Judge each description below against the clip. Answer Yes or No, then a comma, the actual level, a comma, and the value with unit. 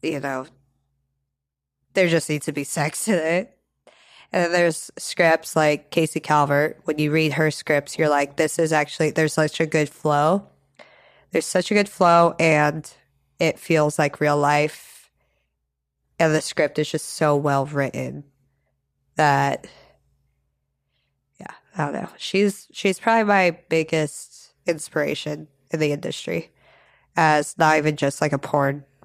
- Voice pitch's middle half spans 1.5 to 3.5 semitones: Yes, narrow, 2.6 semitones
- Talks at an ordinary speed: Yes, average, 150 wpm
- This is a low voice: No, medium, 150 Hz